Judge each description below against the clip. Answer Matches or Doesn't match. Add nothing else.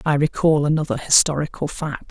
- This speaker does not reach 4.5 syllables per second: Doesn't match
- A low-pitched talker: Doesn't match